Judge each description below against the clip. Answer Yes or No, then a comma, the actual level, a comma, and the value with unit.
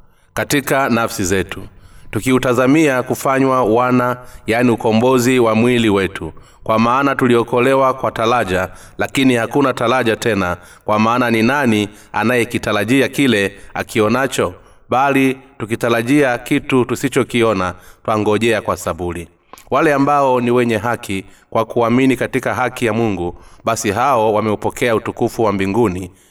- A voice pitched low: Yes, low, 115 Hz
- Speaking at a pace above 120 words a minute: No, average, 115 wpm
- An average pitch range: Yes, average, 3.8 semitones